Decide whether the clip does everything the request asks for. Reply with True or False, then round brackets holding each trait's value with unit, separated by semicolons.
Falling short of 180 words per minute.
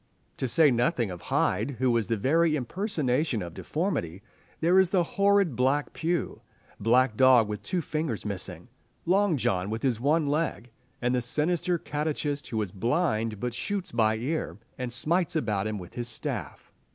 True (170 wpm)